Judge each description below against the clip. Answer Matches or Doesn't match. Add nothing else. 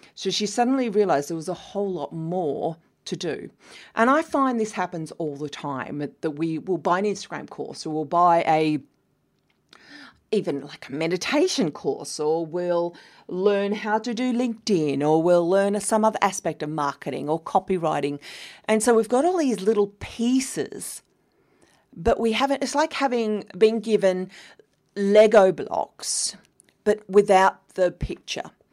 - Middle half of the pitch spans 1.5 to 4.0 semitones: Doesn't match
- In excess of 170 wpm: Doesn't match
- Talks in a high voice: Matches